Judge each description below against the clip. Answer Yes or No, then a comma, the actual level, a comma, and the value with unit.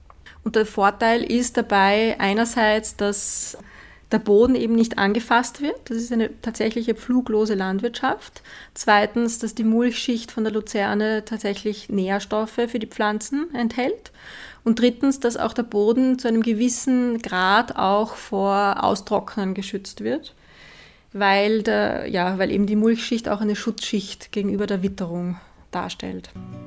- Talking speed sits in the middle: Yes, average, 135 wpm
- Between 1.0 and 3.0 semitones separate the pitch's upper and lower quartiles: Yes, average, 2.7 semitones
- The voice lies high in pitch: Yes, high, 220 Hz